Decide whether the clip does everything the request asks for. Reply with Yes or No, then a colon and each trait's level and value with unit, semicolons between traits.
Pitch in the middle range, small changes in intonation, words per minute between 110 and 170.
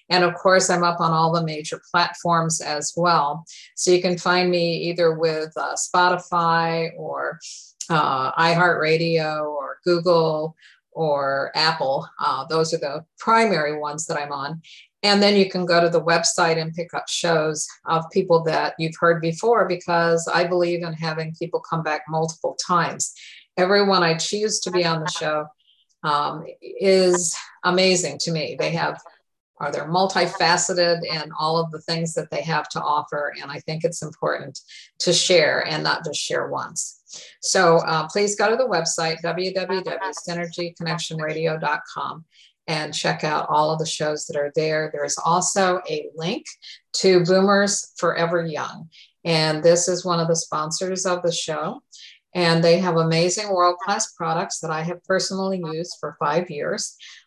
Yes: medium, 170 Hz; narrow, 2.0 semitones; average, 160 wpm